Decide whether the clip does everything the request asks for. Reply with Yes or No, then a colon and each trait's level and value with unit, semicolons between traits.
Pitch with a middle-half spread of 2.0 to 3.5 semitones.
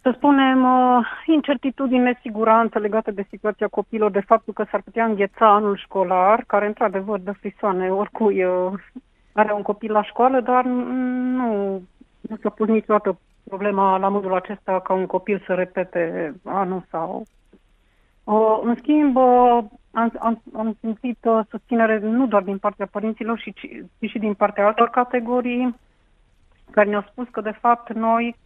Yes: average, 3.1 semitones